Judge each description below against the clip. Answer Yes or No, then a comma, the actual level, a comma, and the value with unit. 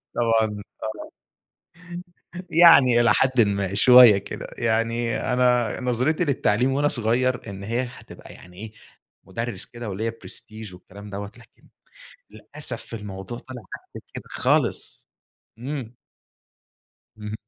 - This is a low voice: Yes, low, 115 Hz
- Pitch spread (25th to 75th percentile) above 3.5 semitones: No, average, 3.2 semitones